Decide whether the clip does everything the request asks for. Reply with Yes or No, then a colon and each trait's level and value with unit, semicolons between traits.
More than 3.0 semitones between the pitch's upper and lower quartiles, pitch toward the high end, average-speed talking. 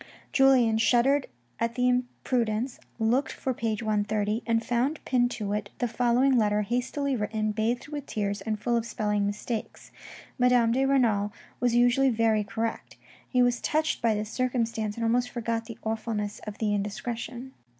No: narrow, 2.5 semitones; high, 230 Hz; average, 160 wpm